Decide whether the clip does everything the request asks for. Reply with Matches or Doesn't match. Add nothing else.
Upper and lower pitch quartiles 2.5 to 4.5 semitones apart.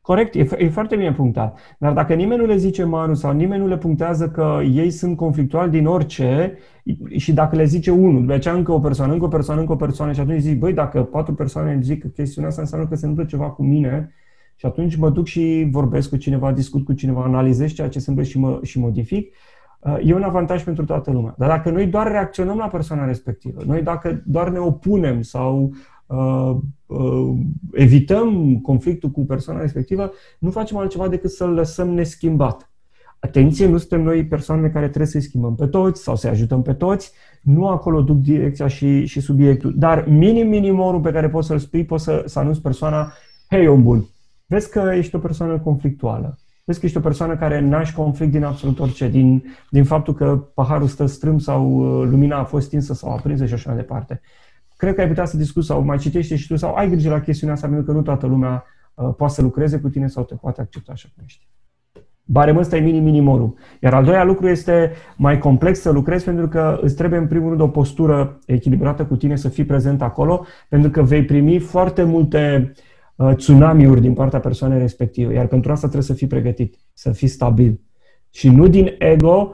Matches